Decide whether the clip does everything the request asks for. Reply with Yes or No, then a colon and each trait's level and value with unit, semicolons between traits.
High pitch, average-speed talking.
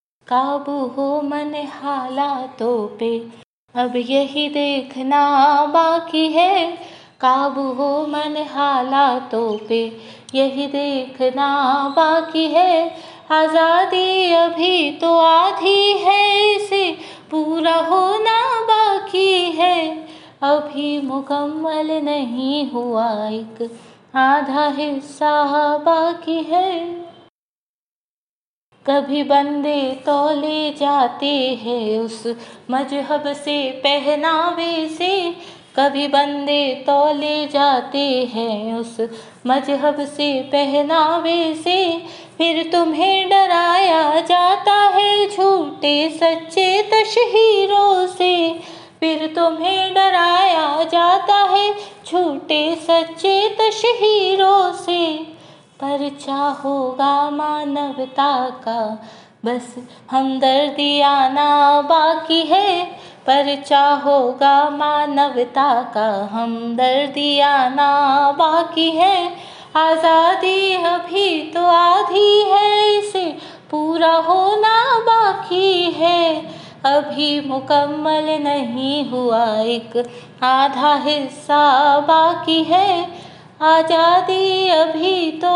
No: very high, 300 Hz; slow, 80 wpm